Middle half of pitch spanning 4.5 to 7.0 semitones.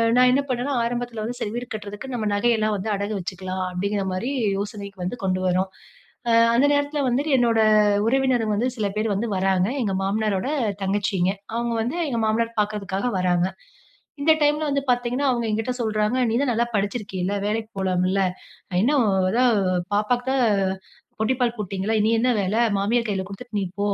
No: average, 3.7 semitones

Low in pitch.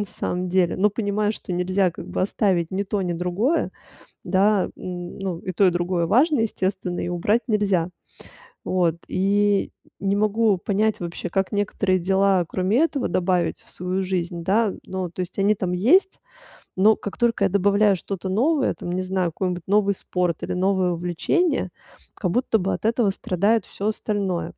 No: high, 190 Hz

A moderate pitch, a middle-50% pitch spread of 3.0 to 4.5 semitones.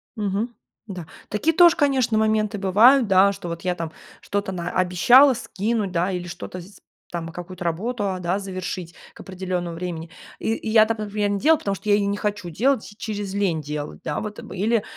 No: high, 200 Hz; average, 3.4 semitones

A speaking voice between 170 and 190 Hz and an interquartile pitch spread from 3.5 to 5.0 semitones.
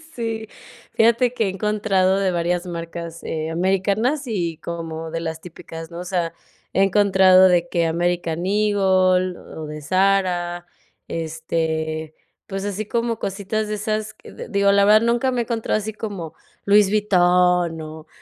Yes: medium, 185 Hz; average, 3.8 semitones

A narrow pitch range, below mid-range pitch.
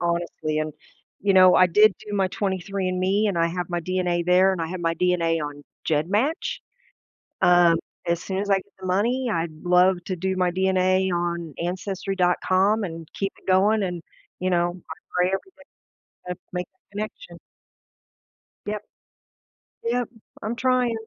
No: narrow, 2.3 semitones; medium, 185 Hz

